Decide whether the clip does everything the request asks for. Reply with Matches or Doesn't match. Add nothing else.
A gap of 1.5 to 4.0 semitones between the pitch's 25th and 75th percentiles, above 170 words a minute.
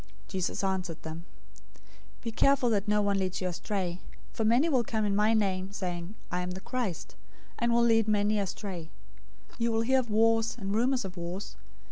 Matches